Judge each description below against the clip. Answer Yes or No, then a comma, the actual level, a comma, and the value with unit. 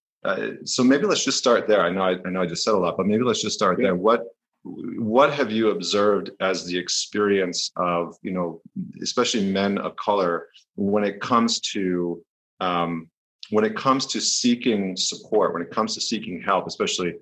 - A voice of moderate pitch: No, very low, 95 Hz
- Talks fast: No, average, 195 wpm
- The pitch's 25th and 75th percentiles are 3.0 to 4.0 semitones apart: Yes, average, 3.3 semitones